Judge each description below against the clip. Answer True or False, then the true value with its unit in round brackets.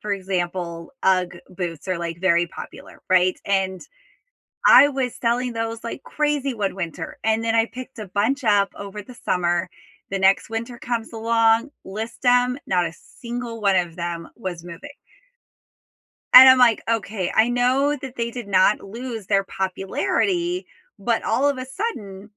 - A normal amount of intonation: True (4.8 semitones)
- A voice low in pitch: False (220 Hz)